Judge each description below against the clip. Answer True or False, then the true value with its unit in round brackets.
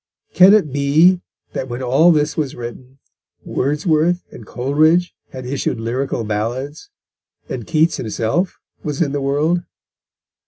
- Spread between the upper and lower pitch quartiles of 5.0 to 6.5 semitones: False (4.2 semitones)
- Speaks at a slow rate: True (130 wpm)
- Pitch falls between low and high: True (145 Hz)